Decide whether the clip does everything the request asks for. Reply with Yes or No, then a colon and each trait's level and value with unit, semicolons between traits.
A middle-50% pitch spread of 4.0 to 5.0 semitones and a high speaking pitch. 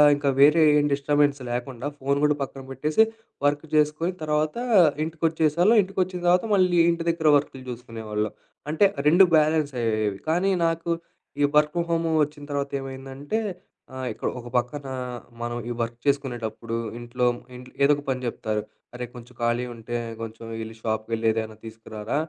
No: average, 4.7 semitones; medium, 140 Hz